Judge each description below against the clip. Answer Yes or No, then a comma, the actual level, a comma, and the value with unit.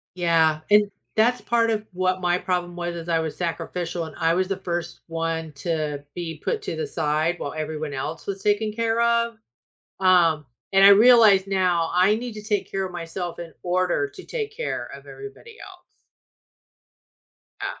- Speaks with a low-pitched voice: No, medium, 180 Hz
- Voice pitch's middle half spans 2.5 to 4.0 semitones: No, average, 4.4 semitones